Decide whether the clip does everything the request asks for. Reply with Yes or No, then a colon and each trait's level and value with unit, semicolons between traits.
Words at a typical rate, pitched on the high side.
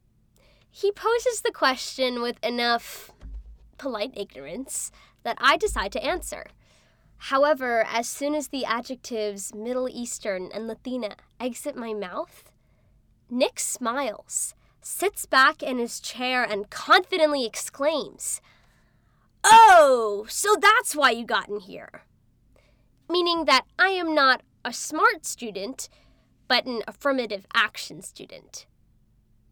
No: slow, 115 wpm; very high, 250 Hz